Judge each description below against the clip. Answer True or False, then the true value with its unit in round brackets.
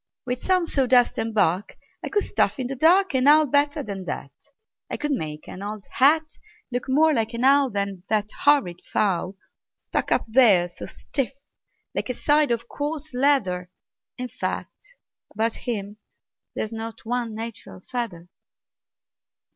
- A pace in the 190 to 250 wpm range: False (155 wpm)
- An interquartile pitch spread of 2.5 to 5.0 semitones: False (5.6 semitones)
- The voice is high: True (245 Hz)